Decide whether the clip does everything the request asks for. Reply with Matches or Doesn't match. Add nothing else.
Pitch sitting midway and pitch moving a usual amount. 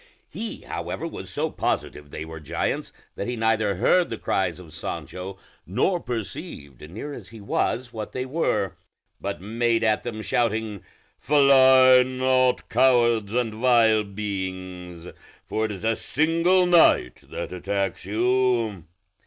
Doesn't match